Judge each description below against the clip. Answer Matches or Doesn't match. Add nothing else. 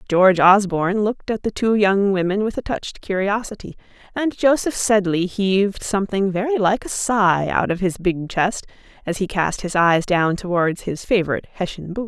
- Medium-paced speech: Matches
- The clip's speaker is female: Matches